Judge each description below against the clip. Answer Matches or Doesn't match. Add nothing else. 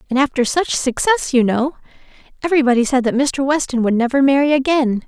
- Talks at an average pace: Matches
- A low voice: Doesn't match